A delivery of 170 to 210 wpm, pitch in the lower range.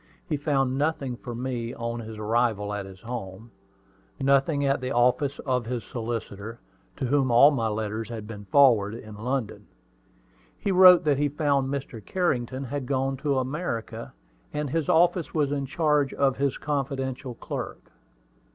No: average, 160 wpm; low, 130 Hz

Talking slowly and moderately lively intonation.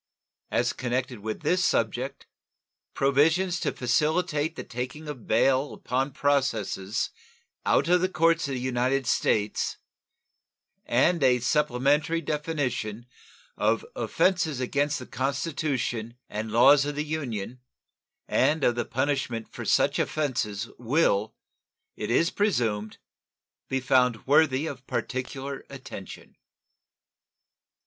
Yes: slow, 115 wpm; average, 3.7 semitones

